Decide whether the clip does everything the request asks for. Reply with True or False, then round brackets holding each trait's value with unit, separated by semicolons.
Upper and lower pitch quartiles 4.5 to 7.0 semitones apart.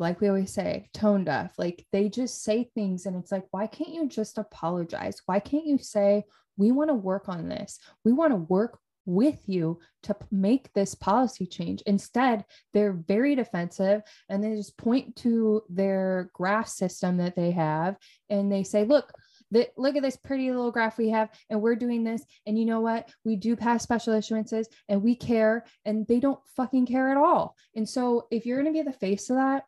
False (3.7 semitones)